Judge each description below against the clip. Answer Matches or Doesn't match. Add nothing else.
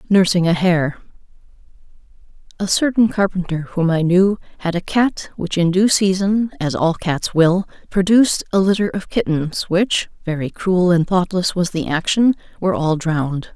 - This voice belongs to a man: Doesn't match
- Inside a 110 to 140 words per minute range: Matches